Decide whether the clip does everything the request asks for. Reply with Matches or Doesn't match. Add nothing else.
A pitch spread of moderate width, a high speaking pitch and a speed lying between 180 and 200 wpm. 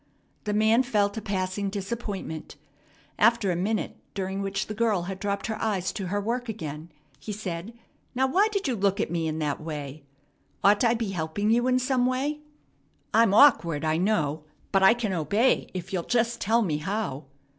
Matches